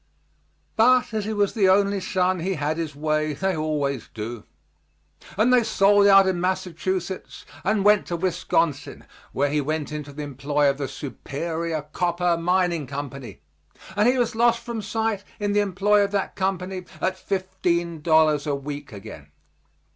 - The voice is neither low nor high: Yes, medium, 175 Hz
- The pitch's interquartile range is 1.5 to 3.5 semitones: No, average, 5.0 semitones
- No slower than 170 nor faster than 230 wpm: No, average, 160 wpm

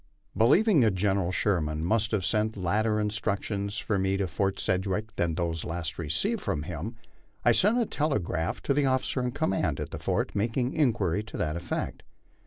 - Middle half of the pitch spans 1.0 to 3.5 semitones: No, average, 4.6 semitones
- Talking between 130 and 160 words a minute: No, average, 180 wpm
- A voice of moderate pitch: No, low, 100 Hz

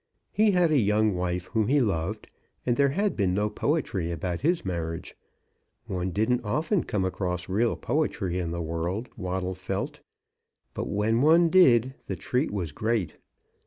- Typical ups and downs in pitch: No, wide, 6.2 semitones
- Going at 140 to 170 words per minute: Yes, average, 160 wpm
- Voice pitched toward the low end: Yes, low, 105 Hz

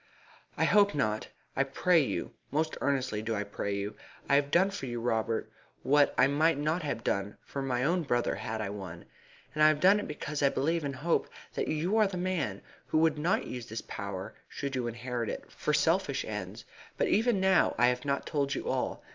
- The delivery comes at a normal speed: No, fast, 215 wpm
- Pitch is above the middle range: No, medium, 140 Hz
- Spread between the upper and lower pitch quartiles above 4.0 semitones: Yes, wide, 5.6 semitones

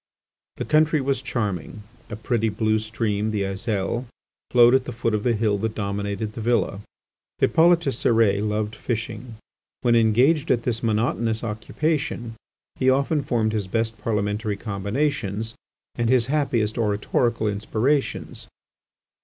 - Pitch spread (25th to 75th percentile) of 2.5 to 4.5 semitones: Yes, average, 2.8 semitones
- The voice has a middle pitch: No, low, 115 Hz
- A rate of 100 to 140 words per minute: Yes, slow, 135 wpm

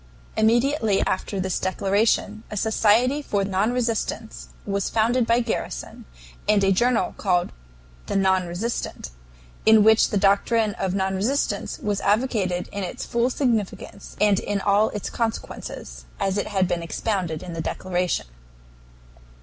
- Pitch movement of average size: Yes, average, 3.1 semitones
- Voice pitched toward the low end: No, high, 205 Hz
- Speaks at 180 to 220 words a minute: No, average, 140 wpm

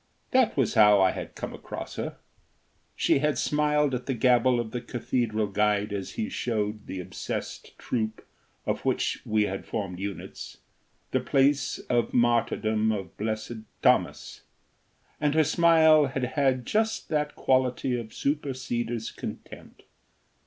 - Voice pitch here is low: Yes, low, 120 Hz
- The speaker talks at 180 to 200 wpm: No, average, 140 wpm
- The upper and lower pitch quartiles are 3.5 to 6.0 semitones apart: Yes, average, 4.6 semitones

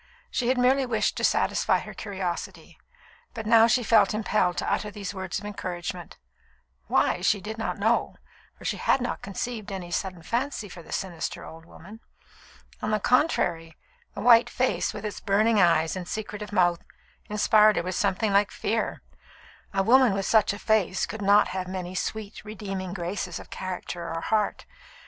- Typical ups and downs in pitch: Yes, average, 3.1 semitones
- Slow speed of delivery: No, average, 175 wpm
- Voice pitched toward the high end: Yes, high, 200 Hz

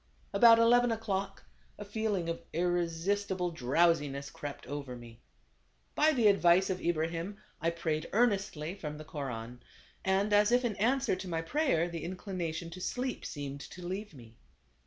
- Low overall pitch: No, medium, 175 Hz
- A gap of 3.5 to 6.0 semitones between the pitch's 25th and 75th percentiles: Yes, average, 4.7 semitones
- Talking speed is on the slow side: No, average, 155 wpm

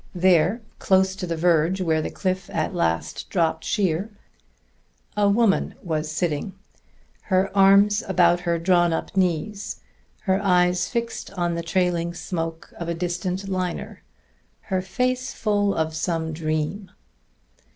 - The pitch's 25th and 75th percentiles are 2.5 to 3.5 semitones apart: Yes, average, 2.8 semitones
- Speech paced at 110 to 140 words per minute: Yes, slow, 135 wpm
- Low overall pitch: No, medium, 180 Hz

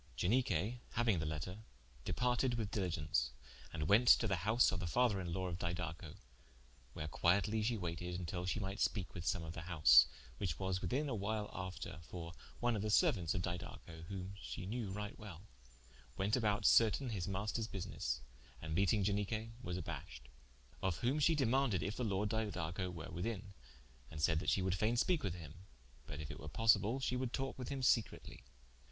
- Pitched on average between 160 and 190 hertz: No, very low, 95 Hz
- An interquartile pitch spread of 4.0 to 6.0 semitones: Yes, average, 4.6 semitones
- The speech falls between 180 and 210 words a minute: Yes, average, 190 wpm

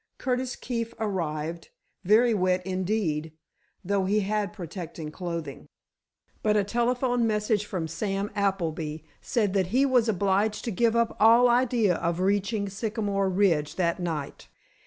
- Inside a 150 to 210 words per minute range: No, slow, 135 wpm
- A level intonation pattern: No, average, 4.0 semitones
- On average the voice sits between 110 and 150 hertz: No, high, 200 Hz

